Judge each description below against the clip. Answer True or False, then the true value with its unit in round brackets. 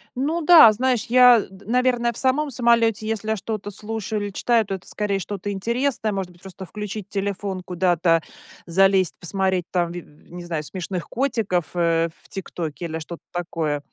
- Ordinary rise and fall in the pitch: True (4.4 semitones)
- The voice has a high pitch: True (195 Hz)